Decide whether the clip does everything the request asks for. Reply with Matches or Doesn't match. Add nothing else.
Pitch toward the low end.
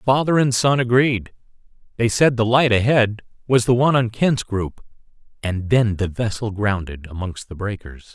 Matches